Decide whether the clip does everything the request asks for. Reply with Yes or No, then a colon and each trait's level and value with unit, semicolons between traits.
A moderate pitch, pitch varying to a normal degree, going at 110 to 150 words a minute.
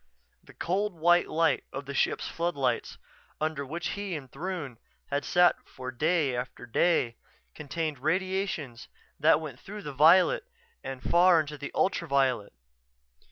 Yes: medium, 155 Hz; average, 4.5 semitones; average, 140 wpm